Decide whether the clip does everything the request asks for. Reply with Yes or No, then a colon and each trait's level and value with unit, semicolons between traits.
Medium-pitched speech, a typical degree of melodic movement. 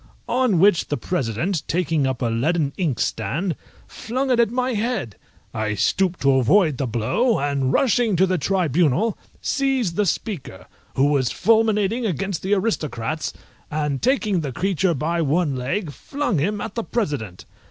No: medium, 175 Hz; wide, 7.1 semitones